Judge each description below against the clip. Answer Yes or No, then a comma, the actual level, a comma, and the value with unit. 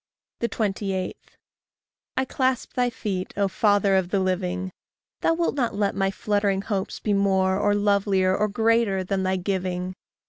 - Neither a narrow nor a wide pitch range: No, narrow, 1.9 semitones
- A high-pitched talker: Yes, high, 200 Hz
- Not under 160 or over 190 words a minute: No, average, 150 wpm